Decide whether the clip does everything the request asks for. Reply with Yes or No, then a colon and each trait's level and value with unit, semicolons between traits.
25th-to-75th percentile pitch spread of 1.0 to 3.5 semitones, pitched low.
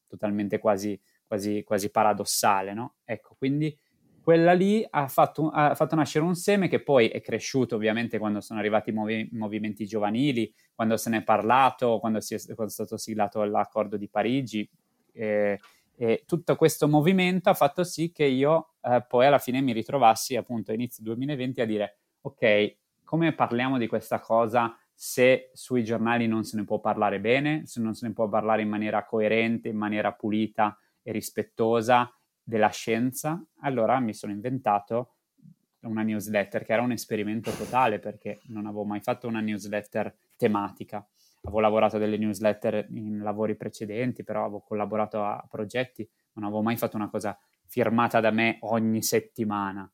Yes: average, 2.8 semitones; low, 110 Hz